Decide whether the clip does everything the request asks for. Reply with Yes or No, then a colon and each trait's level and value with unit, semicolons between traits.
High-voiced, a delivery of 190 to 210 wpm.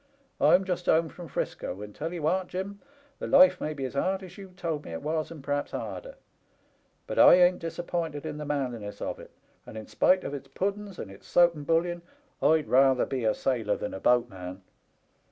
No: medium, 155 Hz; fast, 205 wpm